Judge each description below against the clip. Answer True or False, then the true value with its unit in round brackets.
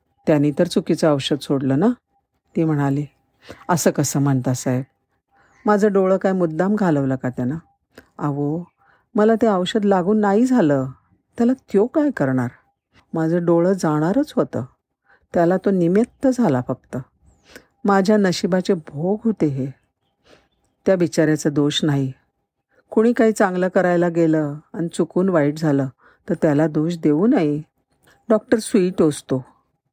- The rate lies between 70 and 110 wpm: False (130 wpm)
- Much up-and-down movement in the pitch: True (6.2 semitones)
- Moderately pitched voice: True (165 Hz)